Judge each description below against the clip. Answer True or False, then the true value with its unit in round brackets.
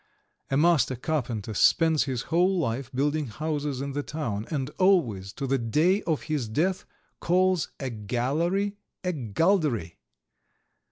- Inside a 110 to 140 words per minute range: True (135 wpm)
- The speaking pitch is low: False (145 Hz)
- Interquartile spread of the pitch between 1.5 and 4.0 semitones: False (5.4 semitones)